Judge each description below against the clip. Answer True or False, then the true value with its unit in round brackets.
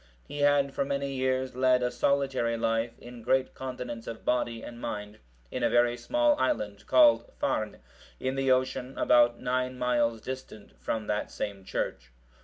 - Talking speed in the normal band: True (165 wpm)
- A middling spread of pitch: False (2.2 semitones)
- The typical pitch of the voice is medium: False (125 Hz)